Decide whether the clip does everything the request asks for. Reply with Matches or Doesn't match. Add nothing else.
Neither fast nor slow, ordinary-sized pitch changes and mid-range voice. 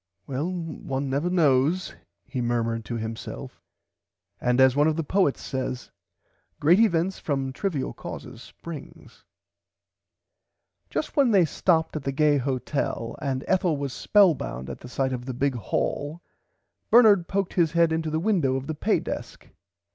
Matches